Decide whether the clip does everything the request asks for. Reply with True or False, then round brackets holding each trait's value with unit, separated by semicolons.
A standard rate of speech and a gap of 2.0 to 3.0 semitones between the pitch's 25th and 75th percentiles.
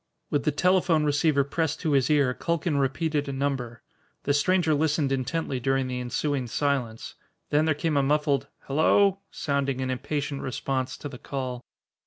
True (165 wpm; 2.5 semitones)